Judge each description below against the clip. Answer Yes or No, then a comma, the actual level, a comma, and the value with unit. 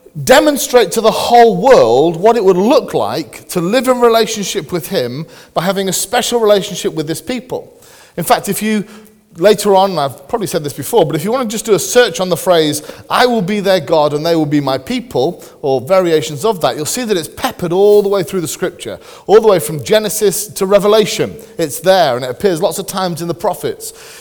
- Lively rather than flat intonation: Yes, wide, 5.8 semitones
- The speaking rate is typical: No, fast, 230 wpm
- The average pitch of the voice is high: Yes, high, 200 Hz